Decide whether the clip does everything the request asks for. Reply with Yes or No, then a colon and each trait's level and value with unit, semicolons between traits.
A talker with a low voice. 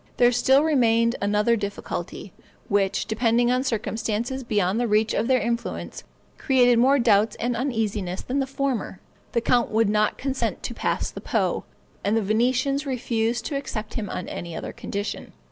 No: high, 230 Hz